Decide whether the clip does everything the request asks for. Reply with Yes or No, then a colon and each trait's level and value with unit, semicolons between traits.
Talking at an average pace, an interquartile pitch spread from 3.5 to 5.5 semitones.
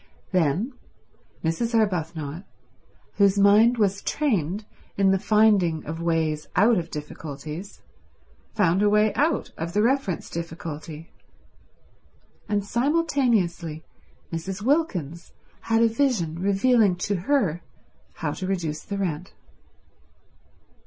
No: slow, 110 wpm; average, 5.1 semitones